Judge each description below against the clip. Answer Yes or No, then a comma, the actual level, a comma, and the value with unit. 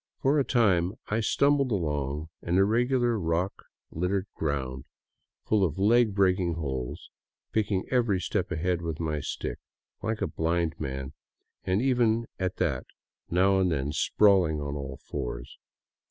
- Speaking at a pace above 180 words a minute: No, average, 140 wpm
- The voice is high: No, very low, 90 Hz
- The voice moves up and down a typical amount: No, wide, 5.8 semitones